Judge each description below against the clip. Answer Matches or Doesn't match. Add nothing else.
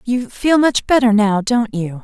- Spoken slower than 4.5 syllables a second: Matches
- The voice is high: Matches